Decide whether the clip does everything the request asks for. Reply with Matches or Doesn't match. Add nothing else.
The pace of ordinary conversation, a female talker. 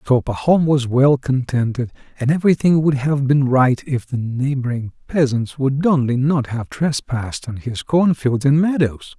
Doesn't match